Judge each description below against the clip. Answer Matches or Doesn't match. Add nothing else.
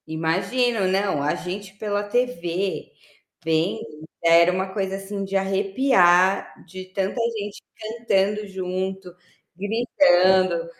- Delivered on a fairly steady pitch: Matches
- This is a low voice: Doesn't match